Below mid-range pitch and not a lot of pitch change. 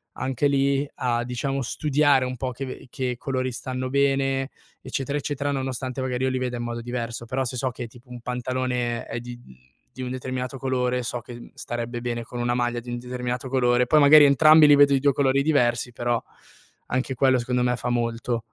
Yes: low, 125 Hz; narrow, 1.8 semitones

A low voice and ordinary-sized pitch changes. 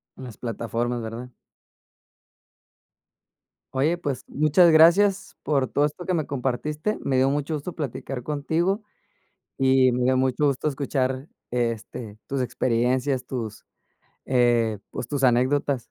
Yes: low, 130 Hz; average, 3.2 semitones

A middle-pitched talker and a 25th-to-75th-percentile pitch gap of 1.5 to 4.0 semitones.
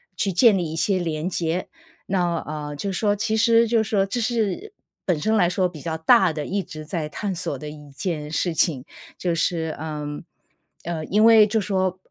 No: medium, 180 Hz; average, 4.6 semitones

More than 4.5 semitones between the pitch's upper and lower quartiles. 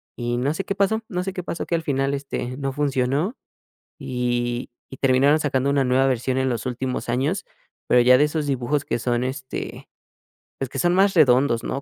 No: average, 3.0 semitones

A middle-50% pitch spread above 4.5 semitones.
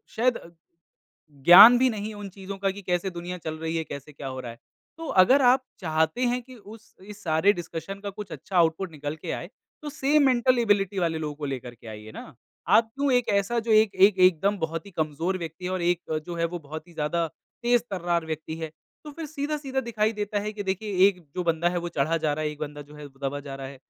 Yes: average, 5.1 semitones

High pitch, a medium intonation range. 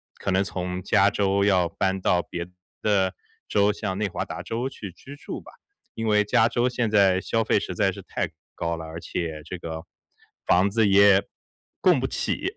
No: low, 100 Hz; average, 3.0 semitones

